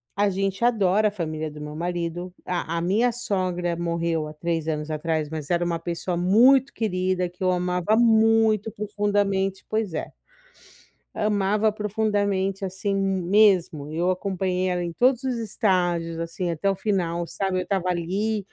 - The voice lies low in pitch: No, medium, 185 Hz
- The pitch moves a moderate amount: Yes, average, 3.3 semitones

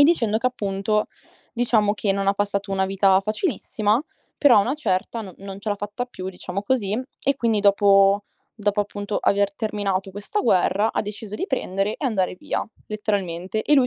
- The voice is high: Yes, high, 205 Hz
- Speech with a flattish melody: Yes, narrow, 2.0 semitones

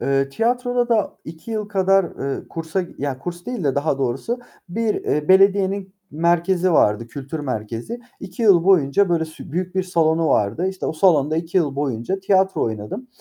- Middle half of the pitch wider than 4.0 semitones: Yes, wide, 5.4 semitones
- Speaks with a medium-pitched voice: Yes, medium, 170 Hz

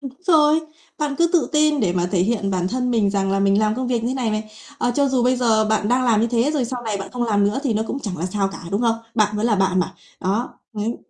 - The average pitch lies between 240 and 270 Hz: No, high, 225 Hz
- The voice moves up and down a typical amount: Yes, average, 4.0 semitones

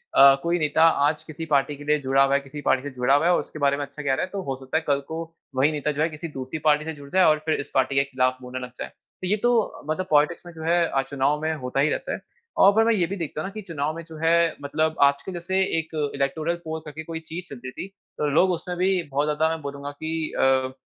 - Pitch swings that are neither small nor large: Yes, average, 3.0 semitones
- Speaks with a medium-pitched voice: Yes, medium, 150 Hz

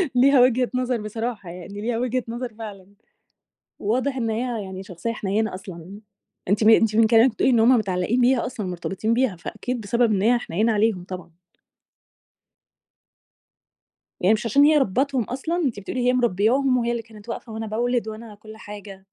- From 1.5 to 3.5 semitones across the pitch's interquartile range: Yes, average, 3.2 semitones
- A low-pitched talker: No, high, 225 Hz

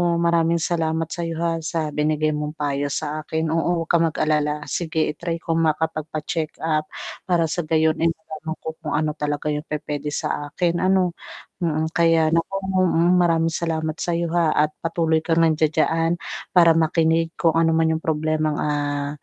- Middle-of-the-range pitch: Yes, medium, 160 Hz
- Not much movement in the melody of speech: Yes, narrow, 1.4 semitones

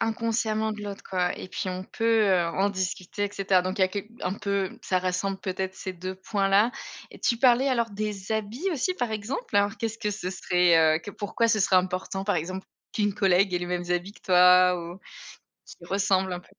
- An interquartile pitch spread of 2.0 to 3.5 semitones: Yes, average, 2.7 semitones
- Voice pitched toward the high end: Yes, high, 195 Hz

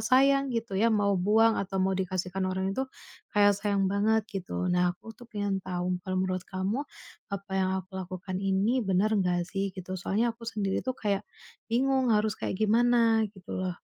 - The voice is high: Yes, high, 195 Hz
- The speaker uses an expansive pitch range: No, average, 3.0 semitones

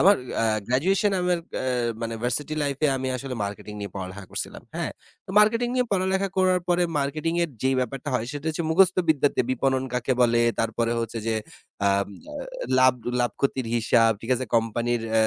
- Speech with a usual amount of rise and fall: No, wide, 6.7 semitones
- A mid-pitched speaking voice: No, low, 130 Hz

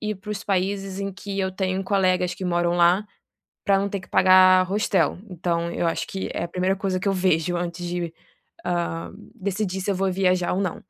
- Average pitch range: No, narrow, 1.7 semitones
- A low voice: No, medium, 185 Hz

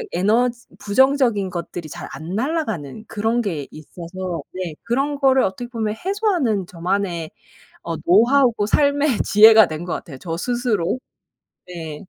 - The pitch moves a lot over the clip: Yes, wide, 6.2 semitones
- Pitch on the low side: No, high, 210 Hz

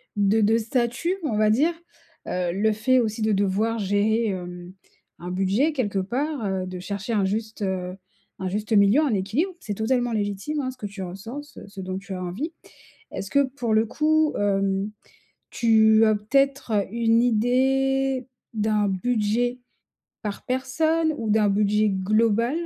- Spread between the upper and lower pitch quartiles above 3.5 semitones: Yes, average, 4.0 semitones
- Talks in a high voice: Yes, high, 220 Hz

